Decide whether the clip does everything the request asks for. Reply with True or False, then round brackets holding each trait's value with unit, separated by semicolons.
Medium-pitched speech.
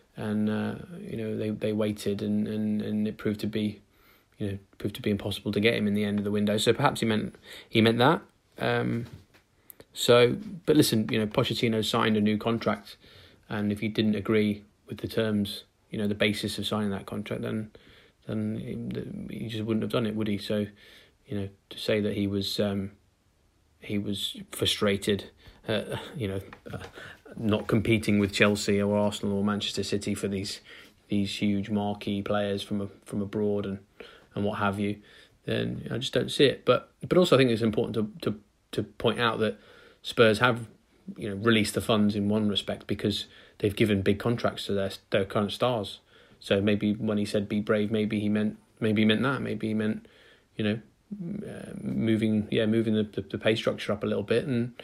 False (105 Hz)